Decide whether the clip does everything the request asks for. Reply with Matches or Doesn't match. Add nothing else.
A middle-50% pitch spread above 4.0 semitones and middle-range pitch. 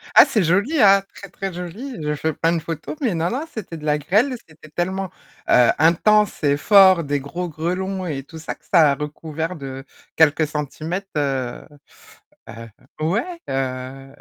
Matches